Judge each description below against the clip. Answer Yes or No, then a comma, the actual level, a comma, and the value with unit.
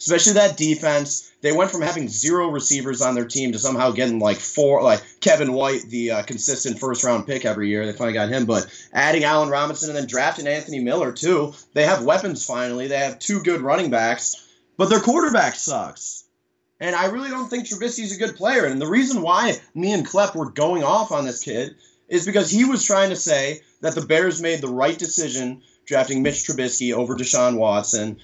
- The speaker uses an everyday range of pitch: No, wide, 5.7 semitones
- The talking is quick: Yes, fast, 210 wpm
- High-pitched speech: No, medium, 140 Hz